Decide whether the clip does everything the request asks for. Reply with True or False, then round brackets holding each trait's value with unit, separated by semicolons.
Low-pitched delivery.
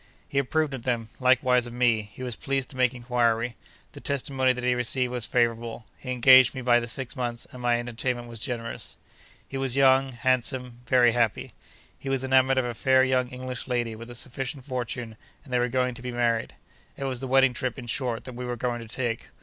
True (125 Hz)